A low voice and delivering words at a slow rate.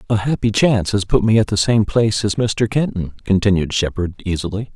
No: low, 105 Hz; average, 200 wpm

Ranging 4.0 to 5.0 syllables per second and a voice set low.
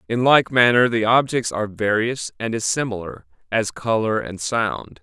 Yes: 4.6 syllables/s; low, 110 Hz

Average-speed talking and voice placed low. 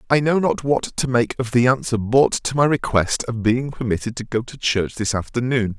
No: fast, 230 wpm; low, 120 Hz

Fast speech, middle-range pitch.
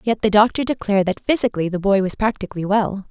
No: fast, 215 wpm; high, 205 Hz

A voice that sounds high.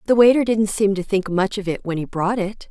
Yes: high, 200 Hz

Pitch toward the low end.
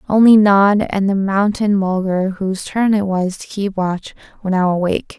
No: high, 195 Hz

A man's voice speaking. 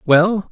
Yes: male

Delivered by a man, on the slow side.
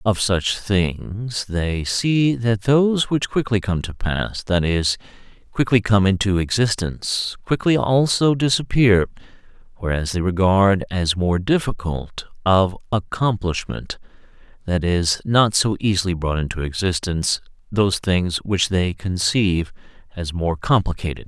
Yes: male; slow, 115 wpm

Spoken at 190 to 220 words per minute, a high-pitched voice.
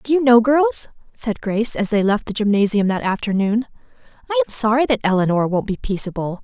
Yes: average, 195 wpm; high, 225 Hz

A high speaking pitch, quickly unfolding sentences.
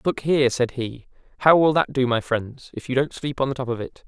No: low, 130 Hz; fast, 265 wpm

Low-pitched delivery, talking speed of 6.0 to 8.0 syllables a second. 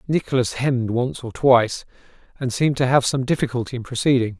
Yes: low, 125 Hz; 6.2 syllables/s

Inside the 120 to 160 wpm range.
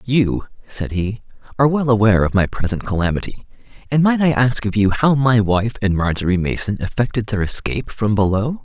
No: average, 190 wpm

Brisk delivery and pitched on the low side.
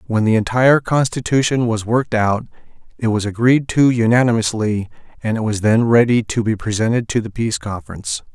No: average, 175 wpm; low, 115 Hz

